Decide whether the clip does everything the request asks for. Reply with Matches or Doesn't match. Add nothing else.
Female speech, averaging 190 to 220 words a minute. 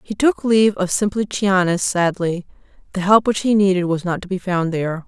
Matches